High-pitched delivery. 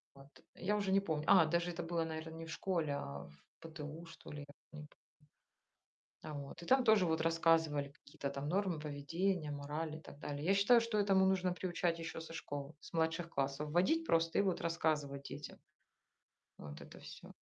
No: medium, 165 Hz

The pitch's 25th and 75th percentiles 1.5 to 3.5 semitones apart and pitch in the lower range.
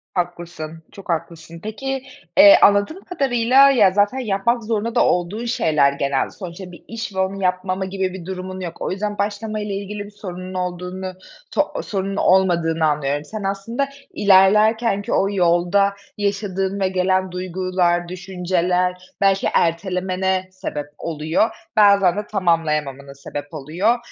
No: average, 2.7 semitones; high, 190 Hz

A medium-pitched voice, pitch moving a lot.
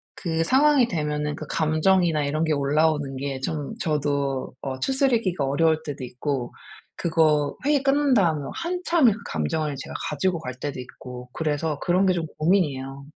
No: medium, 155 Hz; average, 4.7 semitones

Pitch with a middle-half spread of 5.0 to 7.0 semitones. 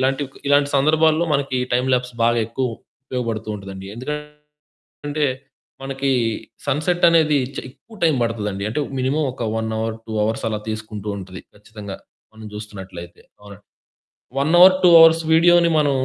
Yes: wide, 5.5 semitones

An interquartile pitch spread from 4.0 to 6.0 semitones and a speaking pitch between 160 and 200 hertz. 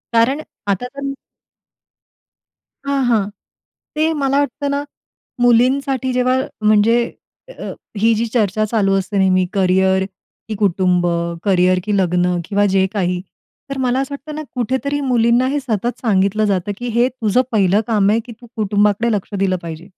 No: average, 4.6 semitones; high, 215 Hz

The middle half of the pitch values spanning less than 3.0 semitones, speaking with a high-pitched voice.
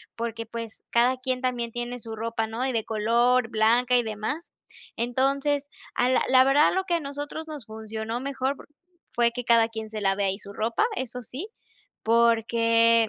Yes: narrow, 2.5 semitones; high, 235 Hz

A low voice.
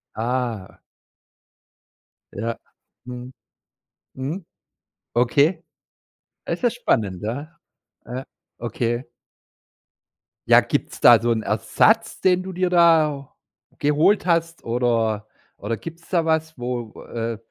Yes: low, 130 Hz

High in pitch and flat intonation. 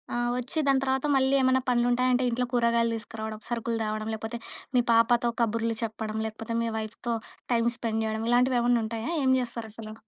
Yes: high, 235 Hz; narrow, 1.7 semitones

